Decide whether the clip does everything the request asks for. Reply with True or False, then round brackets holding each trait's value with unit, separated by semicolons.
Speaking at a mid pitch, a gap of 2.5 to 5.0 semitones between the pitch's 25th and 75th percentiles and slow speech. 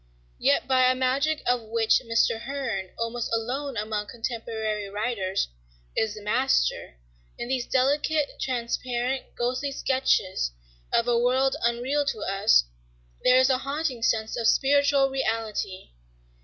False (240 Hz; 3.2 semitones; 130 wpm)